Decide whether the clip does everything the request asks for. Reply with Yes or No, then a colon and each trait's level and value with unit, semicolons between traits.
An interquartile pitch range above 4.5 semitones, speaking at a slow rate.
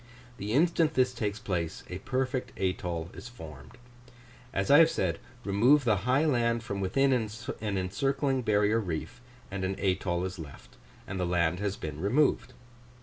No: wide, 5.6 semitones; average, 155 wpm